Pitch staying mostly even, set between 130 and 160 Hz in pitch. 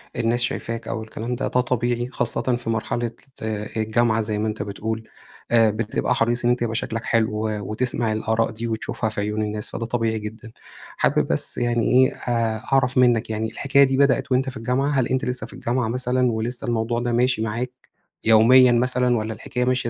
No: narrow, 2.0 semitones; low, 115 Hz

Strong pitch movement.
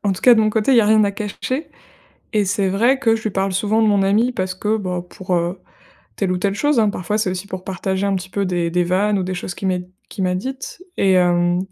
No: average, 2.8 semitones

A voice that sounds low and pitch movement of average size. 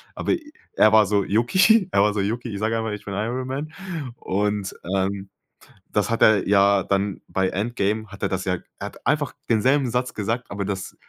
Yes: low, 105 Hz; average, 3.3 semitones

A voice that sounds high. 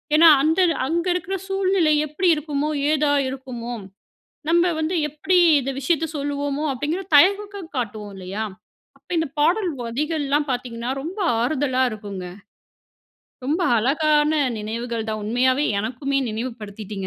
Yes: very high, 285 Hz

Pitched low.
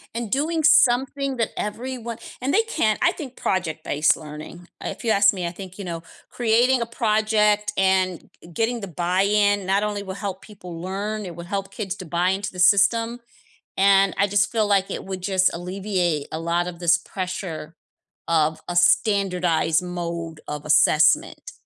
No: high, 195 Hz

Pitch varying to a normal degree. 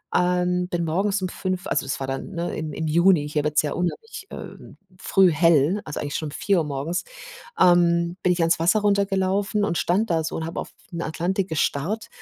Yes: average, 3.3 semitones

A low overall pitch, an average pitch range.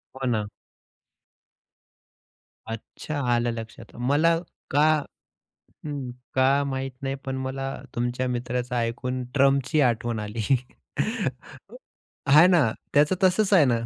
Yes: low, 130 Hz; average, 3.0 semitones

